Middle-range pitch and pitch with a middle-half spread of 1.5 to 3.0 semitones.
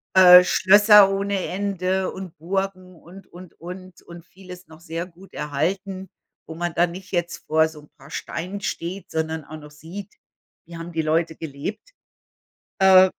Yes: medium, 180 Hz; average, 2.7 semitones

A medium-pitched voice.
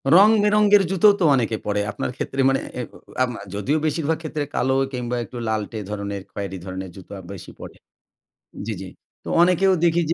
No: low, 130 Hz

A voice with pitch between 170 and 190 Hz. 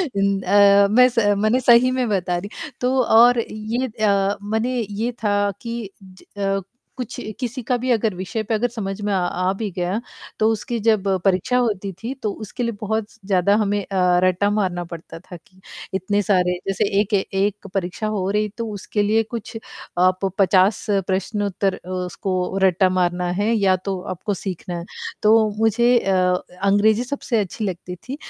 No: high, 205 Hz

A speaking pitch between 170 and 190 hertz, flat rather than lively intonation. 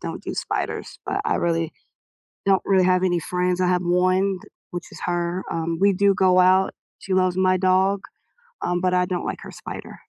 Yes: medium, 185 Hz; narrow, 1.0 semitones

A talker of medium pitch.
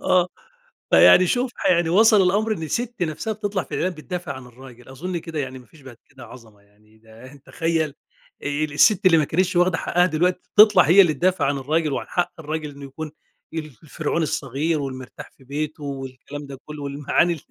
Yes: medium, 155 Hz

